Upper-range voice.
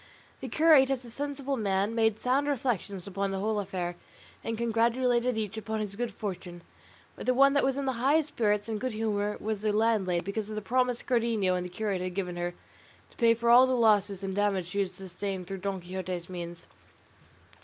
Yes: high, 215 Hz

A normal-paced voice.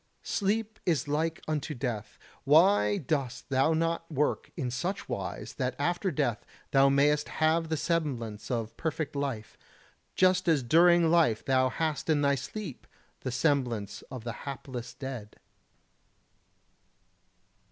No: slow, 130 wpm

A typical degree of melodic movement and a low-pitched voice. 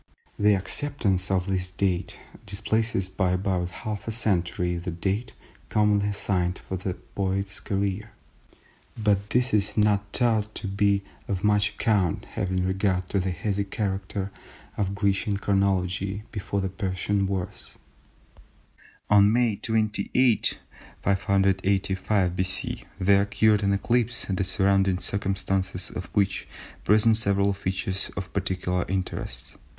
No: narrow, 1.7 semitones; low, 100 Hz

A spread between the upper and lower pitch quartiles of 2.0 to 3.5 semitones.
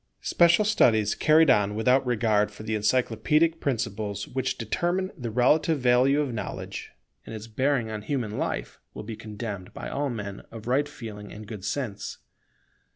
No: average, 4.7 semitones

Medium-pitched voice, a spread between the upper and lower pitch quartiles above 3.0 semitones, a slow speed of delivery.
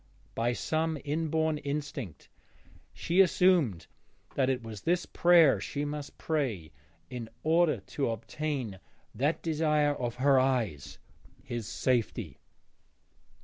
Yes: medium, 145 Hz; average, 4.9 semitones; slow, 110 wpm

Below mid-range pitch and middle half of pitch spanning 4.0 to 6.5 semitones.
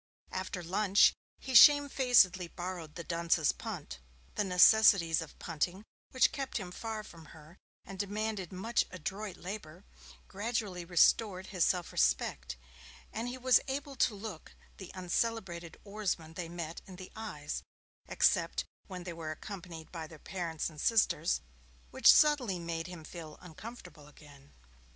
No: medium, 185 Hz; average, 4.4 semitones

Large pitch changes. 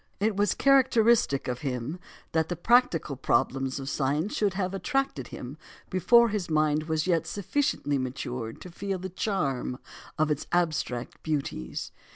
Yes: wide, 6.7 semitones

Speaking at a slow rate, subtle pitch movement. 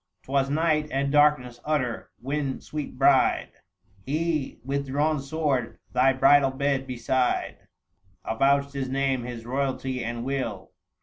Yes: slow, 125 wpm; narrow, 2.0 semitones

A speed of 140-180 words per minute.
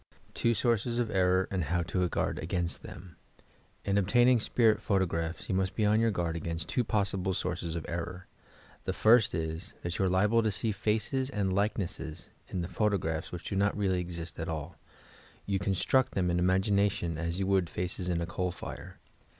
No: average, 195 wpm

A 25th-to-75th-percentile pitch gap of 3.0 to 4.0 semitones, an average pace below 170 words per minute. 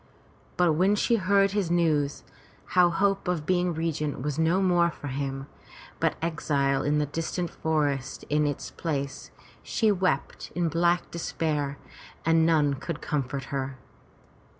Yes: average, 3.6 semitones; average, 145 wpm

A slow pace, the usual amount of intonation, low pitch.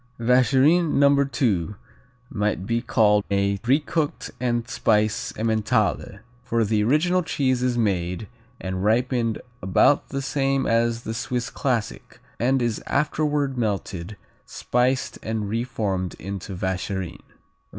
Yes: slow, 120 wpm; average, 4.2 semitones; low, 115 Hz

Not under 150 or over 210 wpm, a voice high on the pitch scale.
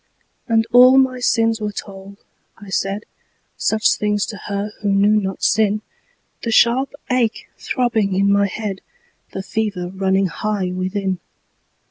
No: average, 140 wpm; high, 205 Hz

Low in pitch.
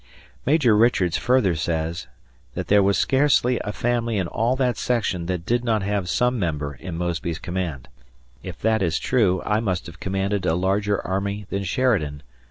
Yes: low, 100 Hz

